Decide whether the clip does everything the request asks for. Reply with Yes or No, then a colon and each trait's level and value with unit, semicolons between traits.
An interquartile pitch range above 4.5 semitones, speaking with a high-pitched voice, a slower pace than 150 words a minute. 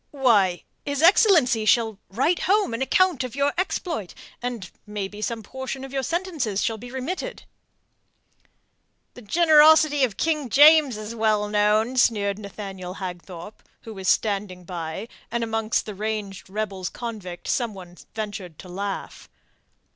Yes: average, 5.1 semitones; high, 220 Hz; average, 140 wpm